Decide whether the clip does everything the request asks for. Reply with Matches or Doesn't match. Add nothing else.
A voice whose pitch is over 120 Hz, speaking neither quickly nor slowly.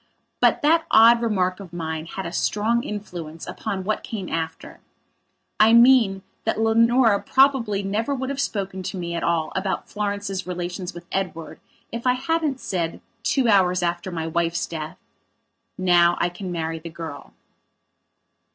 Matches